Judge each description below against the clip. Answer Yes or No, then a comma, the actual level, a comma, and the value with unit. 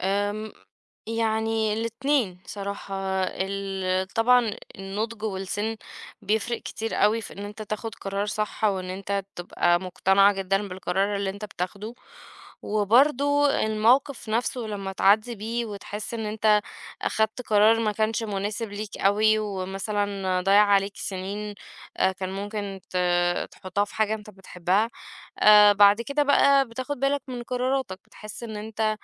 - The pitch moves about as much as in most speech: No, narrow, 2.2 semitones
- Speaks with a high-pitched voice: Yes, high, 210 Hz